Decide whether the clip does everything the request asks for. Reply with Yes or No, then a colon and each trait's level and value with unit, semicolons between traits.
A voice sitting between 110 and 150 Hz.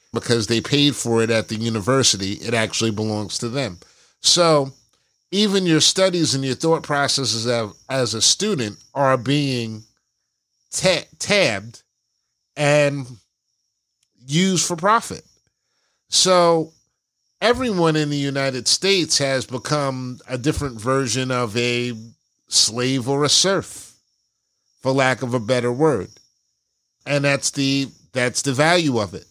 Yes: low, 135 Hz